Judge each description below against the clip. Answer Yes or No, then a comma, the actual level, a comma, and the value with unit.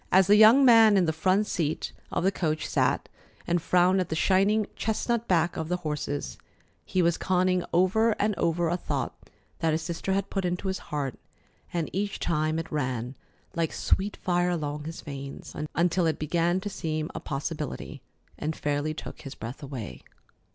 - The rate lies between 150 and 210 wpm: Yes, average, 180 wpm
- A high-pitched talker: No, medium, 170 Hz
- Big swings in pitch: No, average, 3.5 semitones